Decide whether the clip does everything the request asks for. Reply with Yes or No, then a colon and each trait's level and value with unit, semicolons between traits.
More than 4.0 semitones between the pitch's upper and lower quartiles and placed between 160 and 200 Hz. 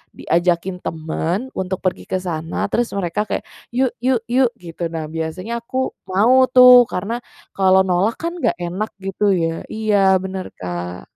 Yes: average, 5.2 semitones; high, 190 Hz